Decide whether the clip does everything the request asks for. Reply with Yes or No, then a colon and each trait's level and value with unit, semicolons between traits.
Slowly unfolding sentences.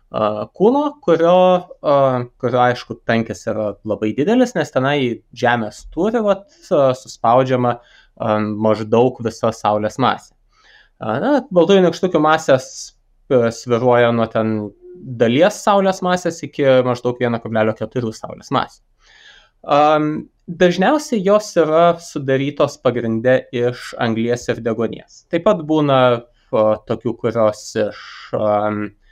Yes: slow, 95 wpm